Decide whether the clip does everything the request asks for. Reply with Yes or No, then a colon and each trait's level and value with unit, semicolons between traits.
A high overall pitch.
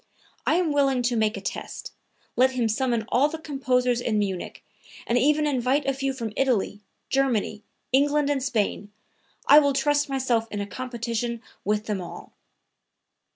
Yes: very high, 255 Hz